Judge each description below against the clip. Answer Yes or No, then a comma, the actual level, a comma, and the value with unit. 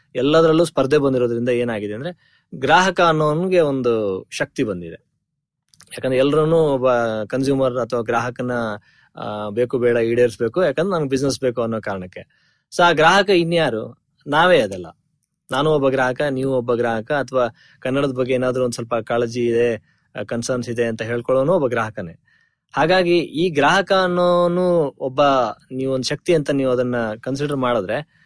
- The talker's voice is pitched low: Yes, low, 130 Hz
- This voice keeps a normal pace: No, fast, 135 wpm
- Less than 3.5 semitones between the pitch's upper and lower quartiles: No, average, 4.2 semitones